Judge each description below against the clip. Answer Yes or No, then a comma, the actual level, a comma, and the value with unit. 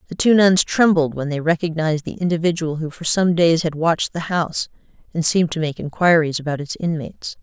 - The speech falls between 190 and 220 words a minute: Yes, average, 200 wpm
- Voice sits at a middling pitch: Yes, medium, 165 Hz